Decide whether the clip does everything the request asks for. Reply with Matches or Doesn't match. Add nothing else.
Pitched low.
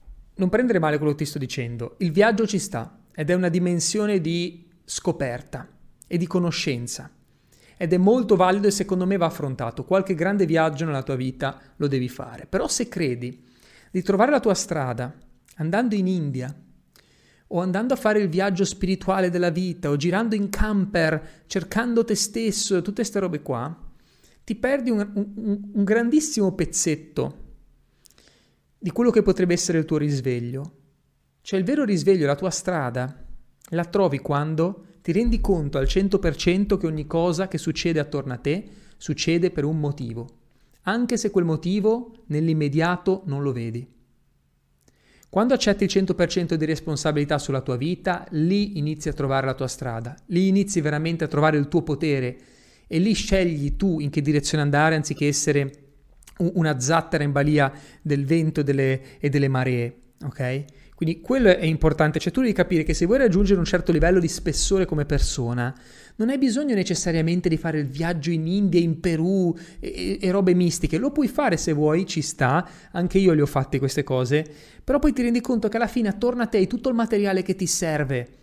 Doesn't match